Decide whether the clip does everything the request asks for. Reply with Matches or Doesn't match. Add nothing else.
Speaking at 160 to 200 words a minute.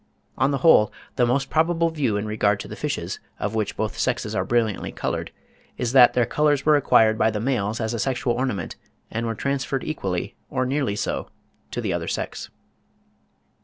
Matches